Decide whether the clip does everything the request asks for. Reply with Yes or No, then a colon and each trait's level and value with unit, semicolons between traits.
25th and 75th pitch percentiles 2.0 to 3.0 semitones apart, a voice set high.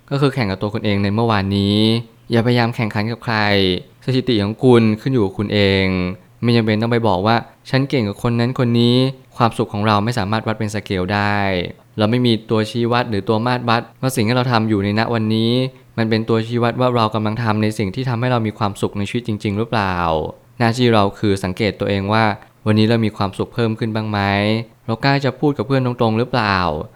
No: narrow, 2.5 semitones; low, 110 Hz